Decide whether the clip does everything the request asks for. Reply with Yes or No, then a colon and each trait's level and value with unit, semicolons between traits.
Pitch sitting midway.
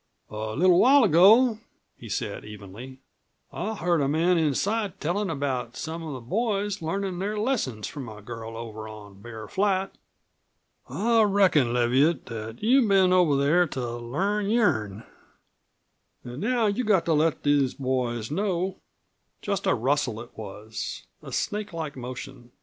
Yes: medium, 150 Hz